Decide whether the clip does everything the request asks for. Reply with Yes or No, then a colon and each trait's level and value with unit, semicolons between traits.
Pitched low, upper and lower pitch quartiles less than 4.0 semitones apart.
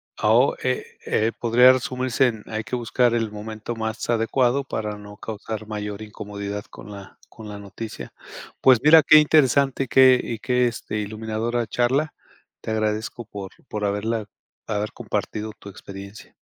Yes: low, 110 Hz; average, 2.9 semitones